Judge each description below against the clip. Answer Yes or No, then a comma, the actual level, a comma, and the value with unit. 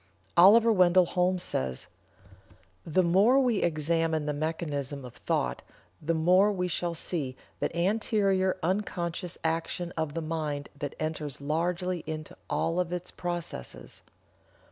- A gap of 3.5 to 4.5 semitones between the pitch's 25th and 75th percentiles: No, average, 2.9 semitones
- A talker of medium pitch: Yes, medium, 170 Hz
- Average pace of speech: No, slow, 130 wpm